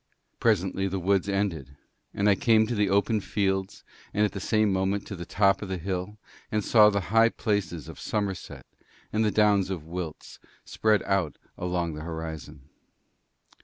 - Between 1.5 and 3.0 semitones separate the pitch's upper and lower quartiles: Yes, average, 2.7 semitones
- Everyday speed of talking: Yes, average, 170 wpm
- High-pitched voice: No, low, 100 Hz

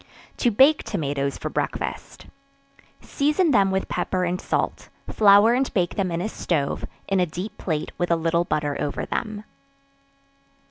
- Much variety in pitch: No, average, 4.4 semitones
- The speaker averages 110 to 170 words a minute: Yes, average, 155 wpm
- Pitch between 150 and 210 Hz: Yes, medium, 185 Hz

